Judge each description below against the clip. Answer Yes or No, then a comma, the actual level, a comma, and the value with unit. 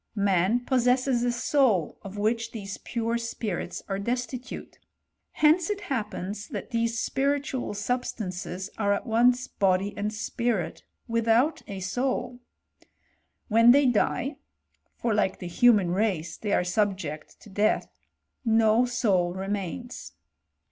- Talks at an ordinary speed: No, slow, 125 wpm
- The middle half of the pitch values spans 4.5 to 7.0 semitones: No, average, 3.8 semitones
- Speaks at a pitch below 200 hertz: No, high, 225 Hz